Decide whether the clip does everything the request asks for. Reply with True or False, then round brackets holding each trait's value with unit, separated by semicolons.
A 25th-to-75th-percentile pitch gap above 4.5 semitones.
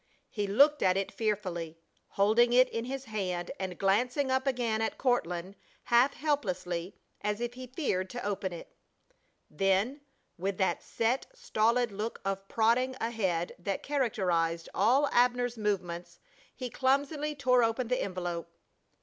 True (5.0 semitones)